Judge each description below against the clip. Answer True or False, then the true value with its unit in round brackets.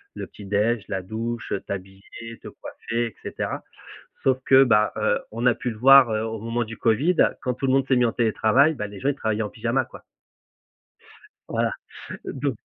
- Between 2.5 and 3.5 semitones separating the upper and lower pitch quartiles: True (2.9 semitones)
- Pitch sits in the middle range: False (115 Hz)